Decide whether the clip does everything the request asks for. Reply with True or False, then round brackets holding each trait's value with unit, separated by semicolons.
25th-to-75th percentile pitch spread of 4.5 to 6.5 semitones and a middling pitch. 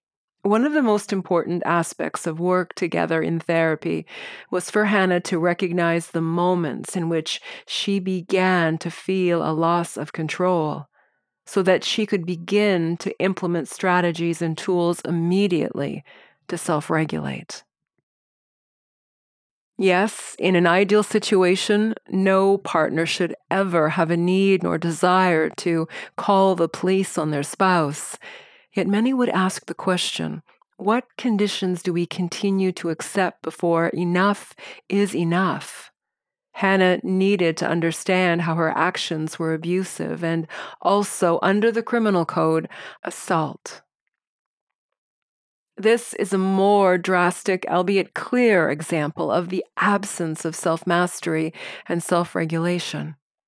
False (2.6 semitones; 180 Hz)